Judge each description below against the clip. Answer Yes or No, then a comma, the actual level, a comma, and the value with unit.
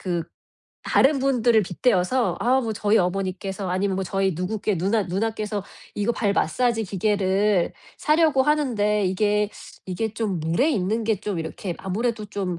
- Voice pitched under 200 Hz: No, high, 205 Hz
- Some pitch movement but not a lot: Yes, average, 3.3 semitones